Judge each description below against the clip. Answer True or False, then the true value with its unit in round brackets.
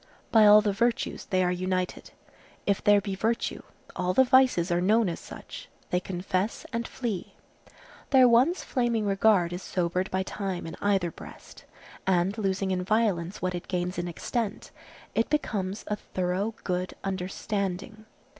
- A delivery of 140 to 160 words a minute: True (155 wpm)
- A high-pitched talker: True (195 Hz)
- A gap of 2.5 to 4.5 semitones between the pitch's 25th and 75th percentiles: True (3.3 semitones)